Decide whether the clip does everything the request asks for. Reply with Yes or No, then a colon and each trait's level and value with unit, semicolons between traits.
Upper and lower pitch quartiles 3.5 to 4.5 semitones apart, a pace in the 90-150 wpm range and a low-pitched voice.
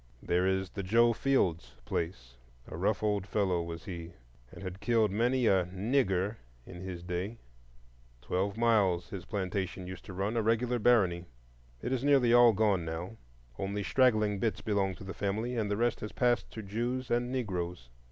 No: average, 4.1 semitones; average, 170 wpm; low, 100 Hz